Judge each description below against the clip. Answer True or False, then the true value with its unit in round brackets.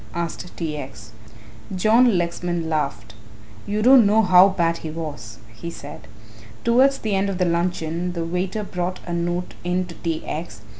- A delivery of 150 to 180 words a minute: True (165 wpm)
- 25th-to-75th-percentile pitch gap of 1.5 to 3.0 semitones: True (2.7 semitones)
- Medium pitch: True (175 Hz)